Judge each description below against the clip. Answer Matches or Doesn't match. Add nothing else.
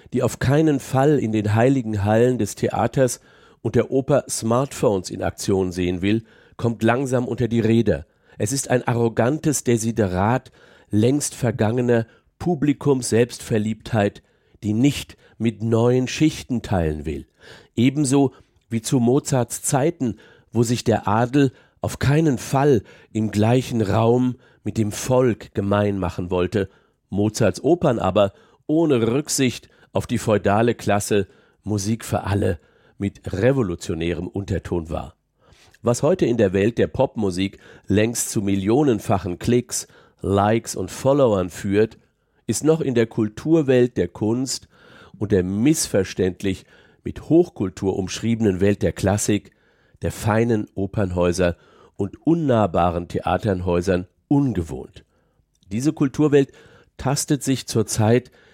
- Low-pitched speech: Matches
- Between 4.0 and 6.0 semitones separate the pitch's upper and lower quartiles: Matches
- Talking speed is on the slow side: Matches